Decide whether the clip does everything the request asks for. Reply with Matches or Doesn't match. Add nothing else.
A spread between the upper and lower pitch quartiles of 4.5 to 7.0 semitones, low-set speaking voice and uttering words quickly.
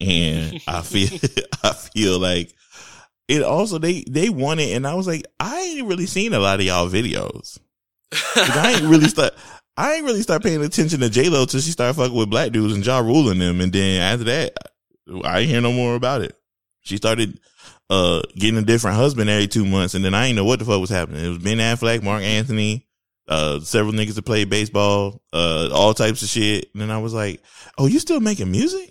Matches